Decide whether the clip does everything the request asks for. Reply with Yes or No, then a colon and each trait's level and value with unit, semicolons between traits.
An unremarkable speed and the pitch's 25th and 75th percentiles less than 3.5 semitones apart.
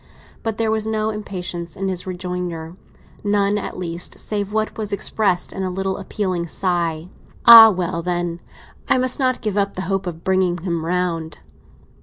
Yes: average, 165 wpm; average, 3.0 semitones